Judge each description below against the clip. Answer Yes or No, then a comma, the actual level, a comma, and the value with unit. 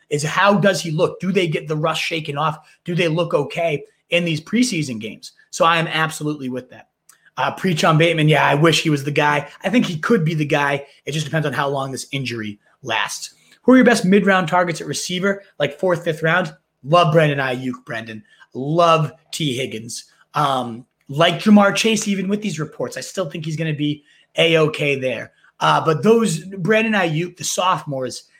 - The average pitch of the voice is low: No, medium, 160 Hz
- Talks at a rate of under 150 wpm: No, fast, 205 wpm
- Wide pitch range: No, average, 3.9 semitones